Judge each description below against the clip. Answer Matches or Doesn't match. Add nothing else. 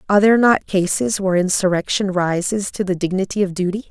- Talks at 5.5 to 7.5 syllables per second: Matches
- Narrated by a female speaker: Matches